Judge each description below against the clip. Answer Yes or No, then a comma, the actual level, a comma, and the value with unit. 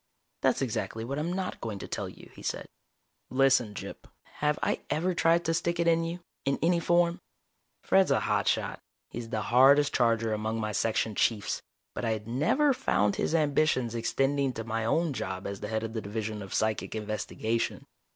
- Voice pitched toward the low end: Yes, low, 120 Hz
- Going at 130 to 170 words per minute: No, average, 190 wpm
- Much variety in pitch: Yes, wide, 6.8 semitones